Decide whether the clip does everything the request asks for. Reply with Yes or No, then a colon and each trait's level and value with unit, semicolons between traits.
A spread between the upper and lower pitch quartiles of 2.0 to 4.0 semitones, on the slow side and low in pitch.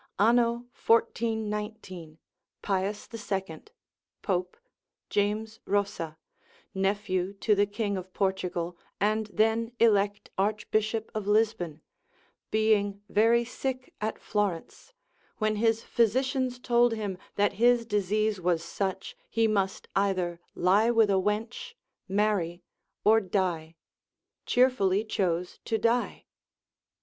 No: average, 2.8 semitones; slow, 105 wpm; high, 210 Hz